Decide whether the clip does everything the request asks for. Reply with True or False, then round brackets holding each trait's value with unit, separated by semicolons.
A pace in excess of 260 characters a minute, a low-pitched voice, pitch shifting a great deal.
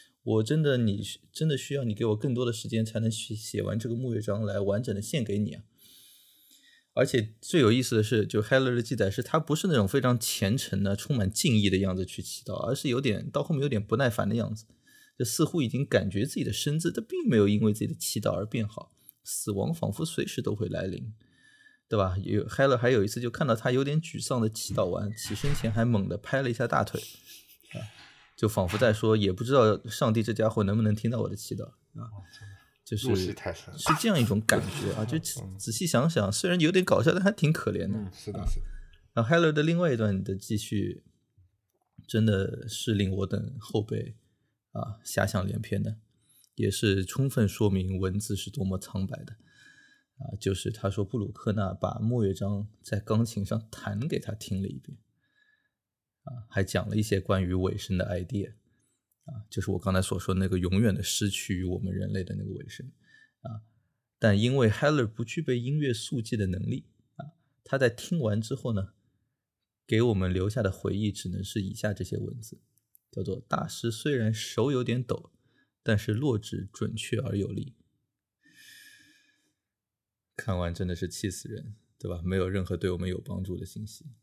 False (295 characters per minute; 110 Hz; 4.0 semitones)